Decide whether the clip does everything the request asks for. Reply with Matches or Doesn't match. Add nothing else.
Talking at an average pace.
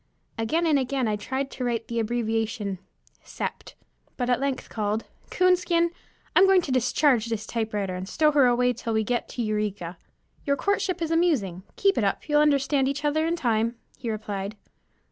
Matches